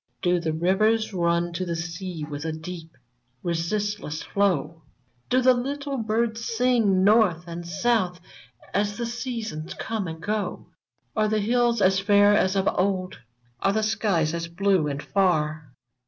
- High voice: Yes, high, 195 Hz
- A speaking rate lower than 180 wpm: Yes, average, 160 wpm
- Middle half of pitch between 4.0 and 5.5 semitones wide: Yes, average, 4.4 semitones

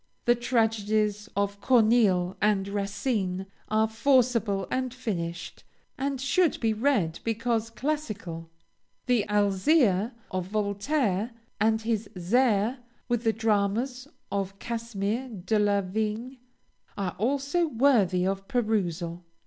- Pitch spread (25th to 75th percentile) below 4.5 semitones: Yes, average, 3.7 semitones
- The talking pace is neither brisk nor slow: No, slow, 110 wpm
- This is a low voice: No, high, 215 Hz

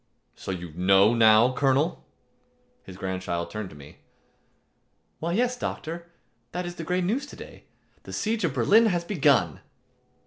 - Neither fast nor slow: Yes, average, 150 wpm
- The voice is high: No, medium, 140 Hz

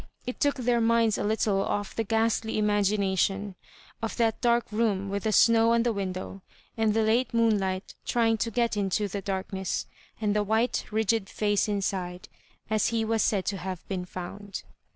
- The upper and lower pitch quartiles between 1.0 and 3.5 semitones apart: Yes, narrow, 2.5 semitones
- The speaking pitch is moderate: No, high, 210 Hz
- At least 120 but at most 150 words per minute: No, average, 180 wpm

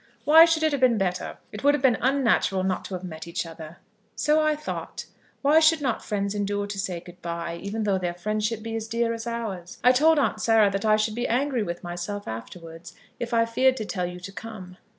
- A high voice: Yes, high, 215 Hz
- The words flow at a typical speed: No, fast, 230 wpm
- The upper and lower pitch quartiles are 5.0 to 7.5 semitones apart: Yes, average, 5.3 semitones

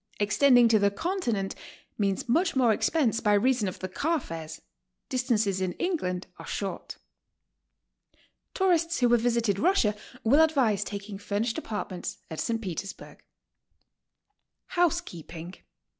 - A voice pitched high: Yes, high, 225 Hz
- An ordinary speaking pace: No, slow, 130 wpm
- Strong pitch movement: Yes, wide, 6.0 semitones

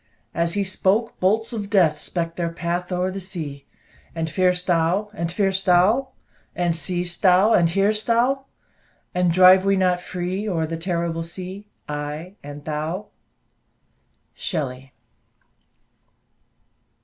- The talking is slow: Yes, slow, 130 wpm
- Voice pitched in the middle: Yes, medium, 180 Hz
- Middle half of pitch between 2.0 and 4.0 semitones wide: Yes, average, 2.7 semitones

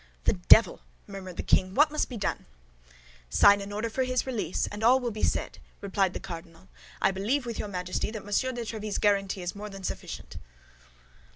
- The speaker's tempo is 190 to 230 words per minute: Yes, average, 195 wpm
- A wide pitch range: No, average, 3.3 semitones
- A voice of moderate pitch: No, high, 205 Hz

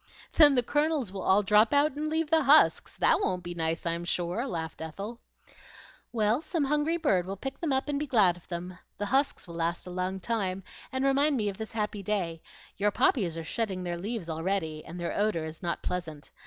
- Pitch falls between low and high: No, high, 200 Hz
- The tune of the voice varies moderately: No, wide, 7.5 semitones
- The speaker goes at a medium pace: No, fast, 215 wpm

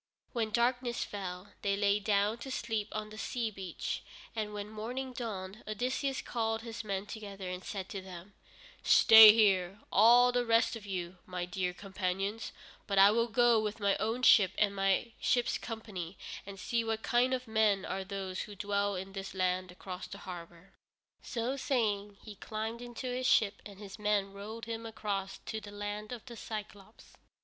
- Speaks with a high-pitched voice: Yes, high, 210 Hz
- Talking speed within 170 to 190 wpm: Yes, average, 180 wpm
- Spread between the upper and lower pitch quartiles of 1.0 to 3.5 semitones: Yes, average, 2.7 semitones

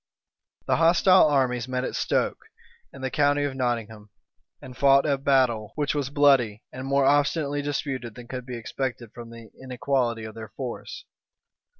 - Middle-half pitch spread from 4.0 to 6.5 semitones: No, average, 3.2 semitones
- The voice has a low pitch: Yes, low, 130 Hz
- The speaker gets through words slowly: No, average, 170 wpm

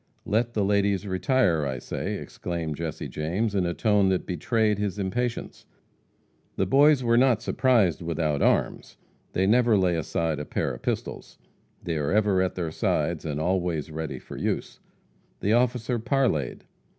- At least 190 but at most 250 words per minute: No, average, 160 wpm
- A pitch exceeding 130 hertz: No, very low, 95 Hz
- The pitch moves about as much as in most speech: No, wide, 5.8 semitones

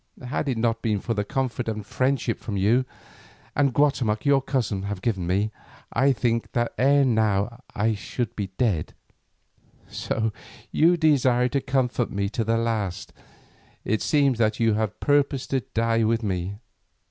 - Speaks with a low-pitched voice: Yes, low, 115 Hz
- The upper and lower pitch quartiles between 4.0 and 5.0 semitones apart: No, average, 3.6 semitones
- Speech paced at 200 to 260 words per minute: No, average, 160 wpm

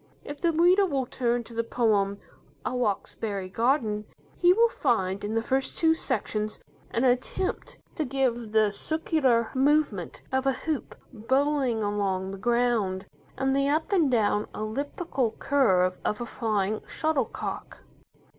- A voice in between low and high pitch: No, high, 240 Hz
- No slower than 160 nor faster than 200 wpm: No, average, 145 wpm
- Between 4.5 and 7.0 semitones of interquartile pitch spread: Yes, average, 5.0 semitones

